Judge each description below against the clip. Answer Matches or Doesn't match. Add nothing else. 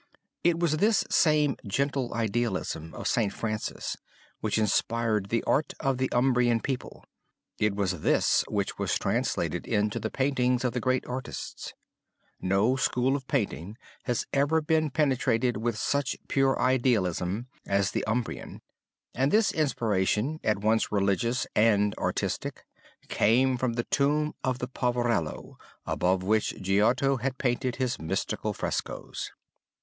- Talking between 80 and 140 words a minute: Matches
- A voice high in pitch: Doesn't match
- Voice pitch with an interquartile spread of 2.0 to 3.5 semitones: Doesn't match